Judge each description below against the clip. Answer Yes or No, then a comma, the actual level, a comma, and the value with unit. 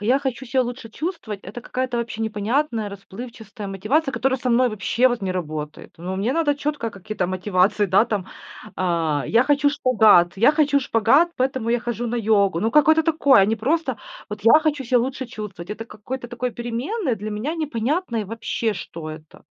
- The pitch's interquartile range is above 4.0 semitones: Yes, average, 4.4 semitones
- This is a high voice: Yes, high, 230 Hz